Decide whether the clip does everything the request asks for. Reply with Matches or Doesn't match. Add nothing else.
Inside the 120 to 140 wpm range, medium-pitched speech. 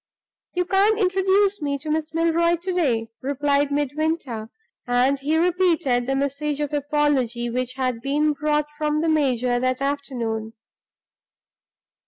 Doesn't match